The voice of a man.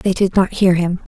No: female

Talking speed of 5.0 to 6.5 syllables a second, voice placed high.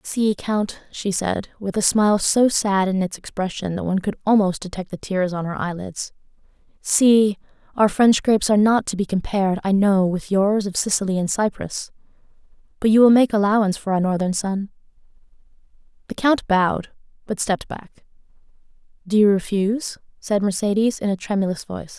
Yes: 5.4 syllables/s; high, 200 Hz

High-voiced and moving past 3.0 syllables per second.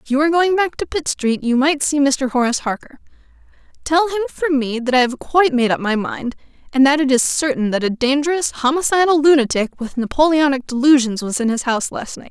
Yes: very high, 275 Hz; 5.9 syllables/s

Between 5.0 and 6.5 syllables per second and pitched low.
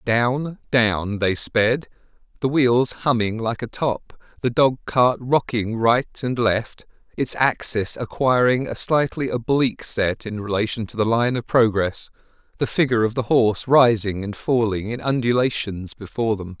No: 4.4 syllables/s; low, 120 Hz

